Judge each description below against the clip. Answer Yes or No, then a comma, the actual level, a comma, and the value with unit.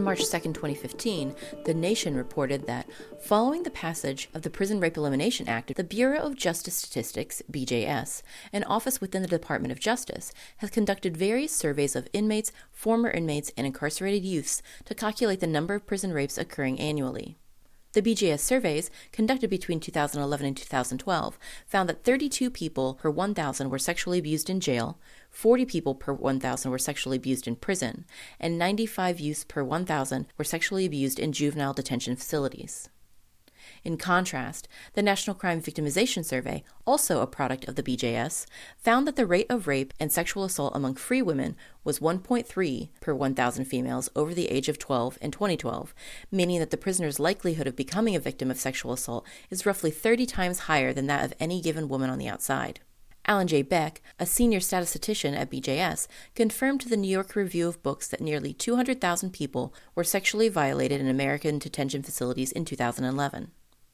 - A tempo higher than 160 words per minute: Yes, average, 170 wpm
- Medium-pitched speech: Yes, medium, 165 Hz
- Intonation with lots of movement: Yes, wide, 6.2 semitones